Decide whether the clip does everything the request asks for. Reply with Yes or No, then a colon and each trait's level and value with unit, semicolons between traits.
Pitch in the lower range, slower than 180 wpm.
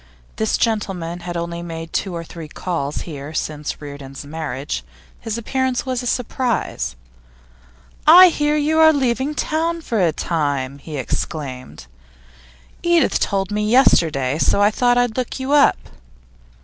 No: high, 190 Hz; average, 145 wpm